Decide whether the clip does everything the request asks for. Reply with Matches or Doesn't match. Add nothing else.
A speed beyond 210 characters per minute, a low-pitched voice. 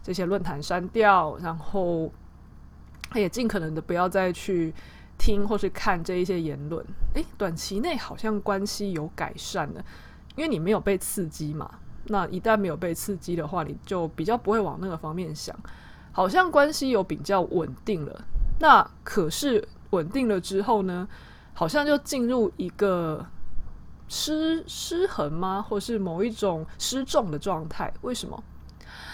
Doesn't match